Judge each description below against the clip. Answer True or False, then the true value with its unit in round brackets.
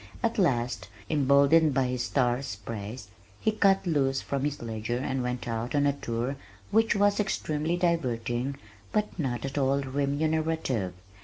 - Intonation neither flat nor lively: True (4.7 semitones)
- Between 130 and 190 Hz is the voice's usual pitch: True (135 Hz)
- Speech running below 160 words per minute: True (150 wpm)